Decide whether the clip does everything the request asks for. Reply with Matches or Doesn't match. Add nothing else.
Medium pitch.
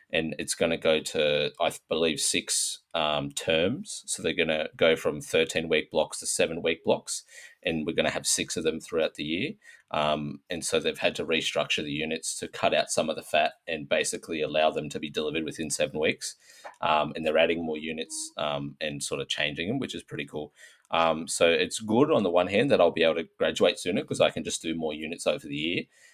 Doesn't match